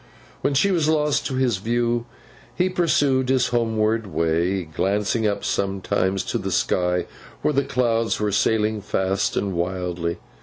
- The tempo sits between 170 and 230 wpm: No, average, 150 wpm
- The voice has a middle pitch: No, low, 110 Hz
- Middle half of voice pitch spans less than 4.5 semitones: No, average, 5.3 semitones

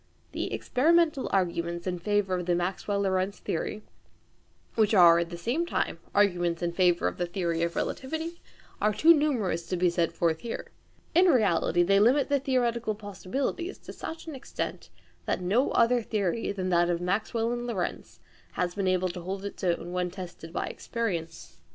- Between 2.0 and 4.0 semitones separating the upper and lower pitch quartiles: No, average, 5.2 semitones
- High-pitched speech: Yes, high, 195 Hz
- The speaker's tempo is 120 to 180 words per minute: Yes, average, 175 wpm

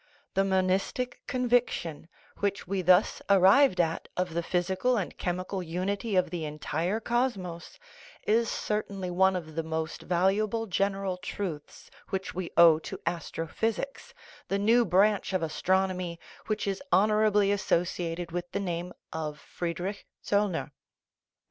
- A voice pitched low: No, medium, 185 Hz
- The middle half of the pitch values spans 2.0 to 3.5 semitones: Yes, average, 2.9 semitones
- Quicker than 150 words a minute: No, slow, 135 wpm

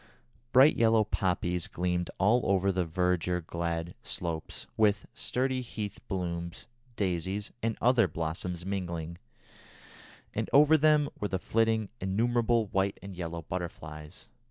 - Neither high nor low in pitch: No, very low, 95 Hz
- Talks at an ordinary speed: No, slow, 120 wpm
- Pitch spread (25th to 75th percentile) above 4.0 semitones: Yes, average, 4.6 semitones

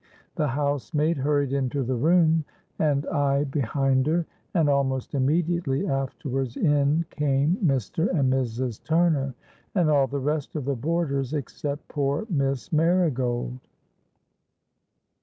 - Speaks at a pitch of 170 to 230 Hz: No, medium, 140 Hz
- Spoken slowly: Yes, slow, 120 wpm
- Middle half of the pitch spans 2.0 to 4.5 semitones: Yes, average, 2.8 semitones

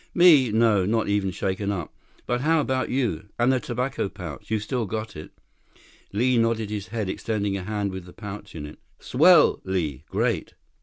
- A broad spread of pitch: No, average, 4.1 semitones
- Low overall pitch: Yes, low, 105 Hz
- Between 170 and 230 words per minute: Yes, average, 185 wpm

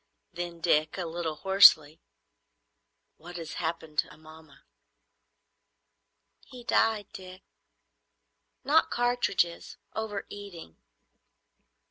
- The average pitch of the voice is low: No, medium, 175 Hz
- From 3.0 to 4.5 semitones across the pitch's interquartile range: Yes, average, 4.1 semitones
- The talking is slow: Yes, slow, 80 wpm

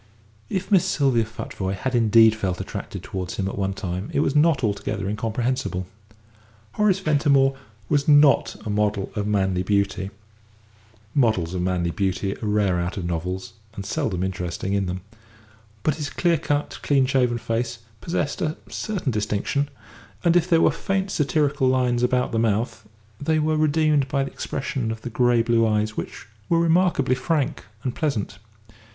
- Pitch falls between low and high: No, low, 120 Hz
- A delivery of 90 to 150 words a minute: No, average, 165 wpm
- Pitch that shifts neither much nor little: No, wide, 6.5 semitones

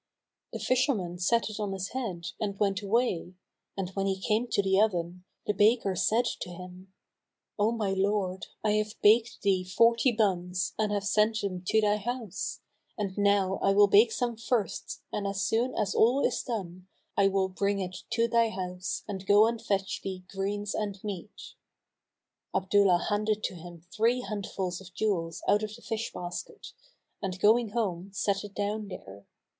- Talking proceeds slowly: No, average, 175 wpm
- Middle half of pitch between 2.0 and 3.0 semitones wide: Yes, narrow, 2.6 semitones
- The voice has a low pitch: No, high, 200 Hz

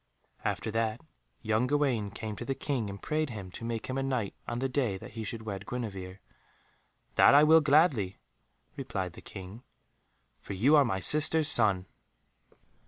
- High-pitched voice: No, low, 115 Hz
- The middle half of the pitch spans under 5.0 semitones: No, wide, 5.4 semitones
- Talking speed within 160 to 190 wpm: Yes, average, 170 wpm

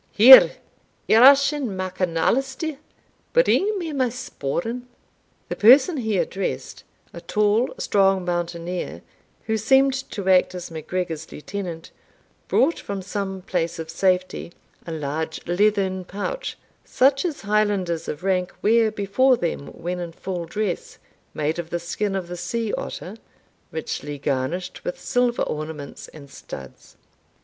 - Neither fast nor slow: No, slow, 130 wpm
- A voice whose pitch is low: No, high, 190 Hz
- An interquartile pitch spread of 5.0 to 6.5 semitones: Yes, average, 5.3 semitones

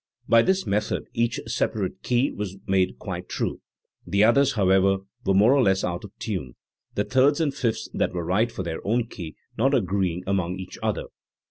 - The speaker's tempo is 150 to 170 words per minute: No, average, 195 wpm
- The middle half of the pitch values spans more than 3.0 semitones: Yes, average, 4.1 semitones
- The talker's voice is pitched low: Yes, low, 100 Hz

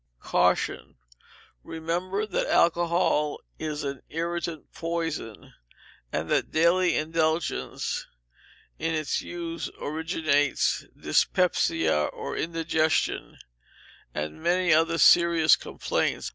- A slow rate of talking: Yes, slow, 90 wpm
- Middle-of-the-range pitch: Yes, medium, 165 Hz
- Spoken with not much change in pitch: Yes, narrow, 1.7 semitones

